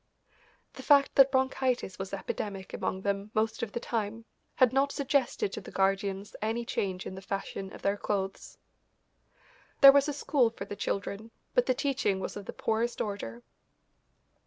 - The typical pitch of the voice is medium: No, high, 215 Hz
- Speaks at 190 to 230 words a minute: No, average, 170 wpm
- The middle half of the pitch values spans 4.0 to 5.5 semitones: Yes, average, 4.7 semitones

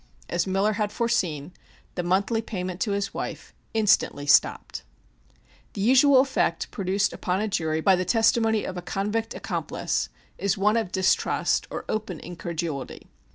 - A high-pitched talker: Yes, high, 195 Hz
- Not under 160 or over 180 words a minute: No, average, 150 wpm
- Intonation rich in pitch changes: No, average, 3.6 semitones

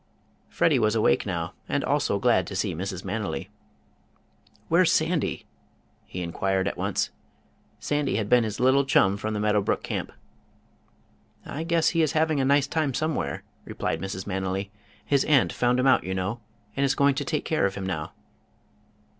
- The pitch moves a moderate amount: No, wide, 6.6 semitones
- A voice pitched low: Yes, low, 110 Hz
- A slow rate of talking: No, average, 175 wpm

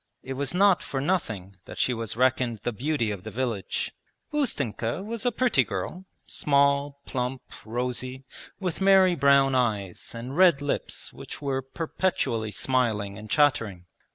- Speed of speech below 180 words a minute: Yes, average, 150 wpm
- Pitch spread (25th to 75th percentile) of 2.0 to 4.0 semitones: No, average, 5.0 semitones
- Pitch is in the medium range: No, low, 130 Hz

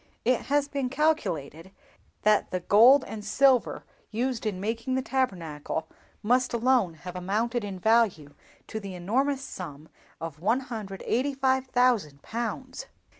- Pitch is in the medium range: No, high, 225 Hz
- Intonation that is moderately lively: No, wide, 5.9 semitones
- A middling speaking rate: No, slow, 125 wpm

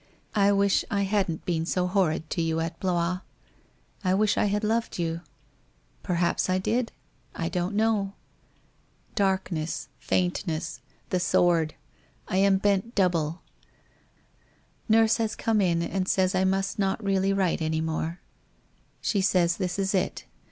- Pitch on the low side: No, medium, 185 Hz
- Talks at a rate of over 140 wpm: Yes, average, 155 wpm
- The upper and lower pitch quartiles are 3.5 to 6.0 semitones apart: No, average, 2.8 semitones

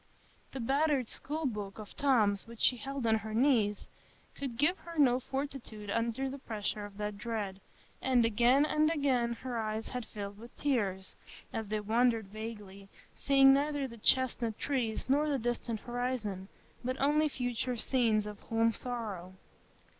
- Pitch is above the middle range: Yes, high, 235 Hz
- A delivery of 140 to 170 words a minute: Yes, average, 160 wpm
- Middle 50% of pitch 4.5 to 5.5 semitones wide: No, average, 3.9 semitones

